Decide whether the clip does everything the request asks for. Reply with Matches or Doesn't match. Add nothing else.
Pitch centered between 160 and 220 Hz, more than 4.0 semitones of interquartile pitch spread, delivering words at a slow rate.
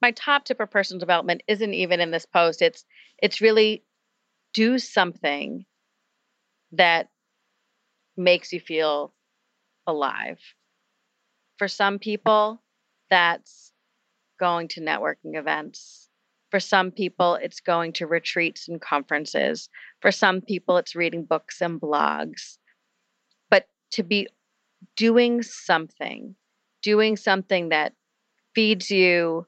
Matches